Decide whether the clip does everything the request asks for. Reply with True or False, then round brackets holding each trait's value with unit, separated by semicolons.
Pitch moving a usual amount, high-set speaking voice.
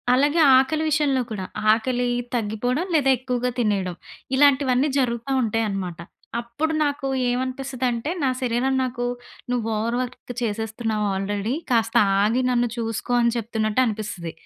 True (3.0 semitones; 240 Hz)